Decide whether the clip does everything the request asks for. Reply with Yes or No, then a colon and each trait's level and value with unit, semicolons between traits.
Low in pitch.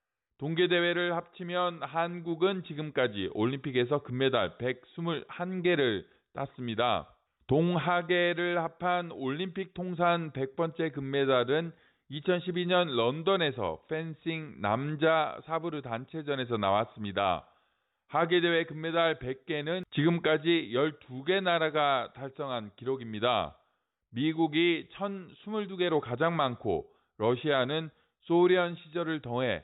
No: medium, 160 Hz